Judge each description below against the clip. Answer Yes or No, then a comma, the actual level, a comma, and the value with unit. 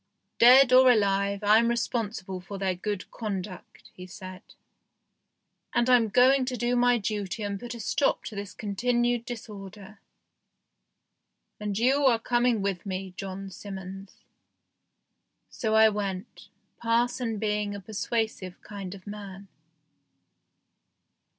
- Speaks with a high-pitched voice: Yes, high, 210 Hz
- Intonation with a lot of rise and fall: No, average, 3.4 semitones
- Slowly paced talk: Yes, slow, 125 wpm